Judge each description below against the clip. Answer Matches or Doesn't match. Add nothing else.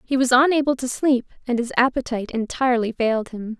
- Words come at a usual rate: Matches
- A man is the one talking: Doesn't match